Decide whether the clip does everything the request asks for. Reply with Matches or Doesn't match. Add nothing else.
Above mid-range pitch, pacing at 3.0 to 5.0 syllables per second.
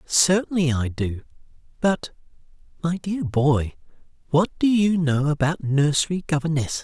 Doesn't match